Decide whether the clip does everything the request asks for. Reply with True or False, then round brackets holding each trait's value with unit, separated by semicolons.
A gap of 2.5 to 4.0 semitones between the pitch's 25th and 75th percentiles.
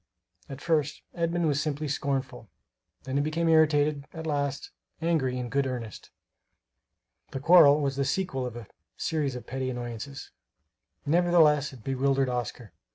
True (2.9 semitones)